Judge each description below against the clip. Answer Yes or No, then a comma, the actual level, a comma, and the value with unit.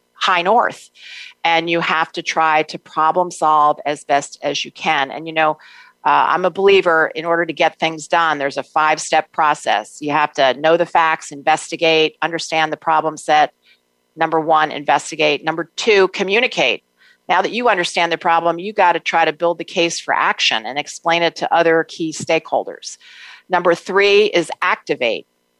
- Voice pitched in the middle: Yes, medium, 165 Hz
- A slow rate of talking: No, average, 180 wpm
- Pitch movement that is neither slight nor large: No, narrow, 1.8 semitones